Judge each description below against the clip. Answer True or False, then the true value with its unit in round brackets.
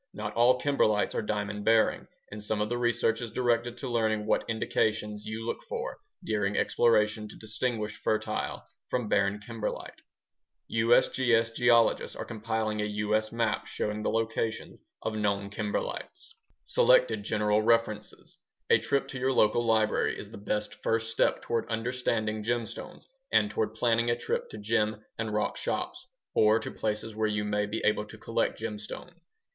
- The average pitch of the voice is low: True (110 Hz)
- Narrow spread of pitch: True (1.8 semitones)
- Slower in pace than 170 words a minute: True (160 wpm)